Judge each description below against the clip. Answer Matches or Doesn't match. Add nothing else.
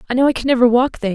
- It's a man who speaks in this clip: Doesn't match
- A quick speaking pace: Matches